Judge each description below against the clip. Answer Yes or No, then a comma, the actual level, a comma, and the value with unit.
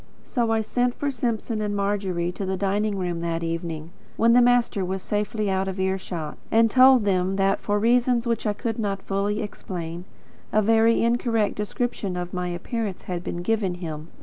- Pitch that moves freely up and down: No, average, 3.9 semitones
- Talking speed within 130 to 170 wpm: No, average, 190 wpm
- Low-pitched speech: No, high, 200 Hz